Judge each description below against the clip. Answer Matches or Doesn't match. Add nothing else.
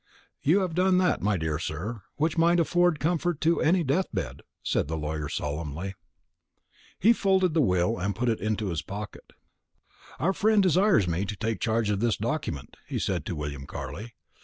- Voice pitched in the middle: Doesn't match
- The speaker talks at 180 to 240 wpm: Matches